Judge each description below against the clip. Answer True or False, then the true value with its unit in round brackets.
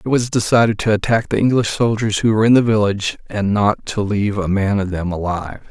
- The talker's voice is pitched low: True (105 Hz)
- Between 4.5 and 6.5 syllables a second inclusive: True (6.0 syllables/s)